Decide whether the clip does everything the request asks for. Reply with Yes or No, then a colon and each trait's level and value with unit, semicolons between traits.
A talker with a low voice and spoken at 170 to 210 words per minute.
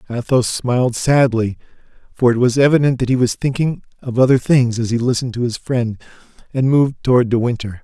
Yes: low, 125 Hz; average, 190 wpm